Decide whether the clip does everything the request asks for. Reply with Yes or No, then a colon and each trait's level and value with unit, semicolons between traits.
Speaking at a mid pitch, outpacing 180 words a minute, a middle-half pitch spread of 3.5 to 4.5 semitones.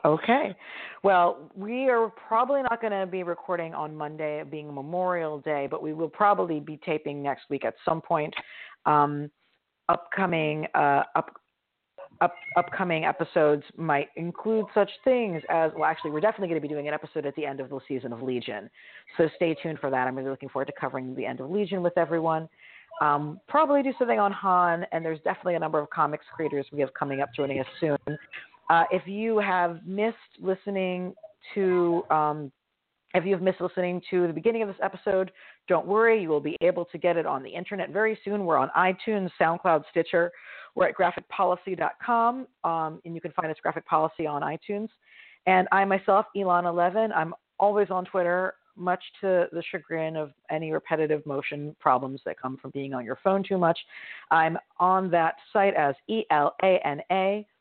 Yes: medium, 170 Hz; average, 190 wpm; average, 4.2 semitones